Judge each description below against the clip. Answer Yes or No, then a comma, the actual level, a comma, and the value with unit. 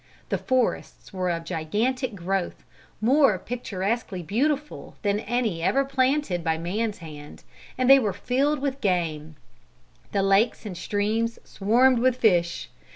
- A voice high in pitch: Yes, high, 215 Hz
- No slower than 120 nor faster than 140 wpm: Yes, slow, 135 wpm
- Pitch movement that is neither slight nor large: No, wide, 6.0 semitones